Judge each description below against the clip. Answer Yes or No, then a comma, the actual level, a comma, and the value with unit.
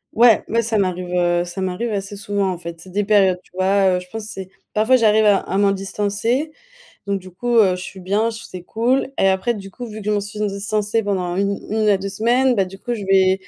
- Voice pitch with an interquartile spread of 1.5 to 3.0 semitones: Yes, narrow, 2.5 semitones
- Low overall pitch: No, high, 200 Hz